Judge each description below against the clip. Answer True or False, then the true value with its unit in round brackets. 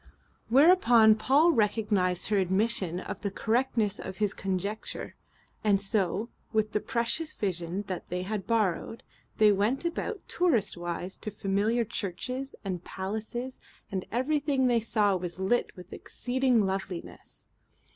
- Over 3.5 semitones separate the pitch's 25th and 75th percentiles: True (4.1 semitones)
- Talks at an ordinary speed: False (130 wpm)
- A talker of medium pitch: False (215 Hz)